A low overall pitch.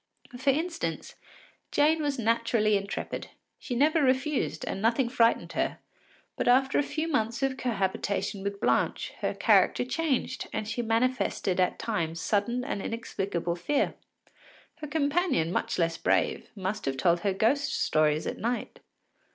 No: high, 230 Hz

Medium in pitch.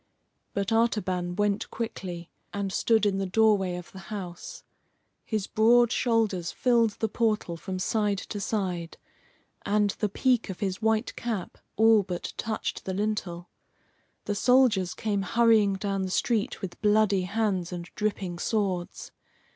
No: high, 205 Hz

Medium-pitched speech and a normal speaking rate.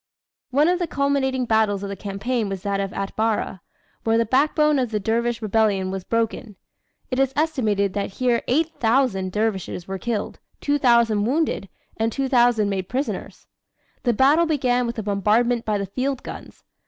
No: high, 230 Hz; average, 165 wpm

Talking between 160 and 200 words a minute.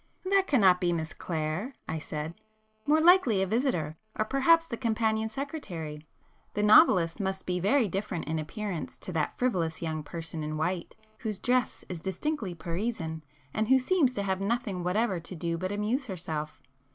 Yes: average, 165 wpm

